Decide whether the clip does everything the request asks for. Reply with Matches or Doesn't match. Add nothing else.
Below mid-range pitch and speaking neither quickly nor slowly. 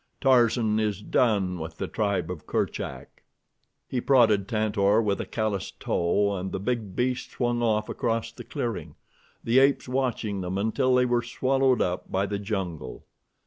Matches